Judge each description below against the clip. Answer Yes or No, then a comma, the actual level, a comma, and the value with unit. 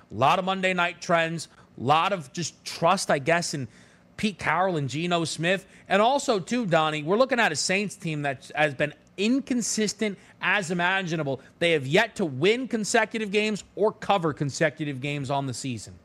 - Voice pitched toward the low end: No, medium, 175 Hz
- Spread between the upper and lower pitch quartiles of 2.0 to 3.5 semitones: No, wide, 5.4 semitones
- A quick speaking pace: No, average, 185 wpm